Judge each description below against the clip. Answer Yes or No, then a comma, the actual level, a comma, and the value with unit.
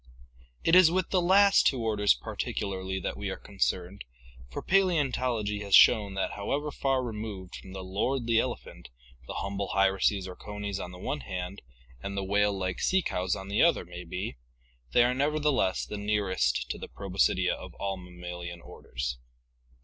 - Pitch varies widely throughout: No, average, 5.0 semitones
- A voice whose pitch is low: Yes, low, 100 Hz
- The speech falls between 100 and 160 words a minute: No, average, 170 wpm